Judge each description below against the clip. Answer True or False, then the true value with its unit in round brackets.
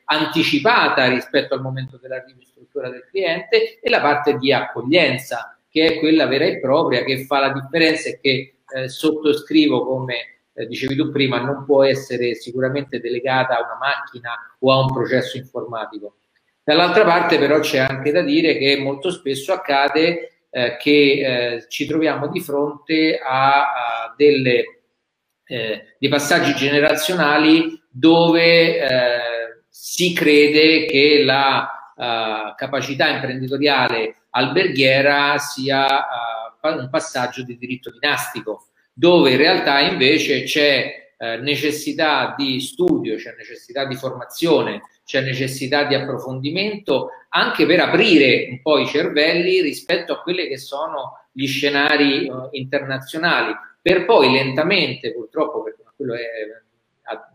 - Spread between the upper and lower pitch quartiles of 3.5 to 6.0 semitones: False (3.1 semitones)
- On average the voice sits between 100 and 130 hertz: False (140 Hz)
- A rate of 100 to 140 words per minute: True (135 wpm)